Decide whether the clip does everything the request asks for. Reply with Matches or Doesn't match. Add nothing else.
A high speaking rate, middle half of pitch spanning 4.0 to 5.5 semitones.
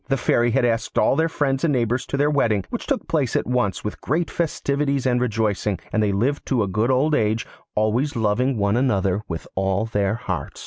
Matches